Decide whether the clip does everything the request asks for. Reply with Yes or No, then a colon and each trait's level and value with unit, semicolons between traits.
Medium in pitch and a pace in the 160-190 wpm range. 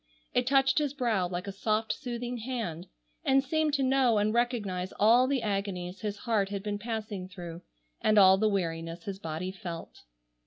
No: high, 210 Hz; average, 180 wpm